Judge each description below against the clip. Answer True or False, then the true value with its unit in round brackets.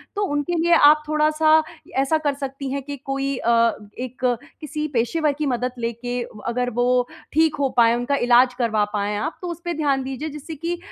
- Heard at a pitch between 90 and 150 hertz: False (275 Hz)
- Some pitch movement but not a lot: True (3.8 semitones)